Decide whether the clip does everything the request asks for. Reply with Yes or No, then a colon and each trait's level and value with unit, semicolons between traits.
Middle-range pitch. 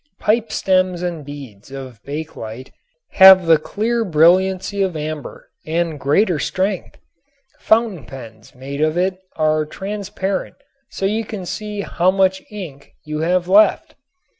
Yes: medium, 175 Hz